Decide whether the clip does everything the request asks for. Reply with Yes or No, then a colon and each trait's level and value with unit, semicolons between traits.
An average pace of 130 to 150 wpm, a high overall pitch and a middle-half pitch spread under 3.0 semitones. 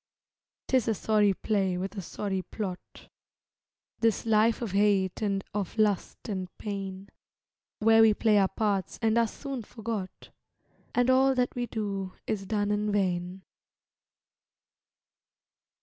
Yes: slow, 135 wpm; high, 210 Hz; narrow, 2.5 semitones